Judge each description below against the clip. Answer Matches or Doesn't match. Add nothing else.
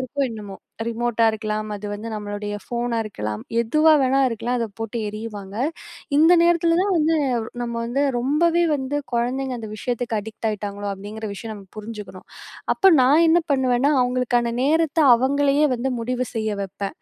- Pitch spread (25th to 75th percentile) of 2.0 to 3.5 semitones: Doesn't match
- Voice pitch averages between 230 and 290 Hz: Matches